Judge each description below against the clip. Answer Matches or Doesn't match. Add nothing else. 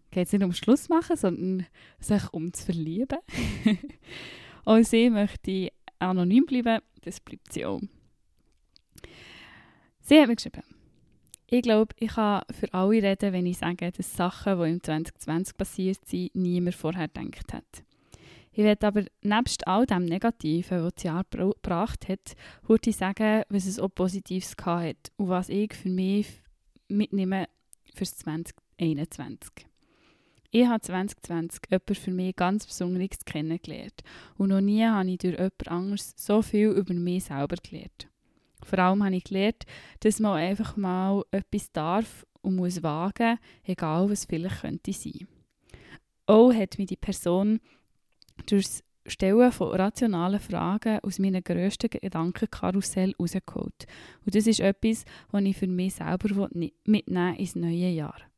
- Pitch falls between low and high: Doesn't match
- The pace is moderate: Matches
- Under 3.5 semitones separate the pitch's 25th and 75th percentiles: Matches